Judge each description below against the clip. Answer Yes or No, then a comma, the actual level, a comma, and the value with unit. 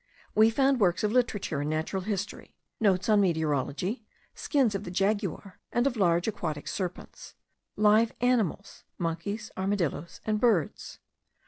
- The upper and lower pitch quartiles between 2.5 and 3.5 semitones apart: No, average, 4.0 semitones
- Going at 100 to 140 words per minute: Yes, slow, 135 wpm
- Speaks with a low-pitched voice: No, high, 200 Hz